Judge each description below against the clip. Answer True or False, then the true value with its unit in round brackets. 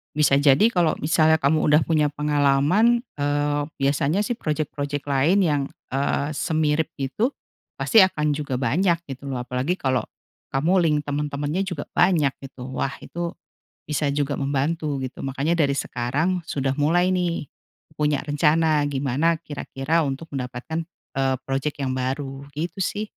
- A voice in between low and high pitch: True (145 Hz)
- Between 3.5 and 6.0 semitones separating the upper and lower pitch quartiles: False (2.9 semitones)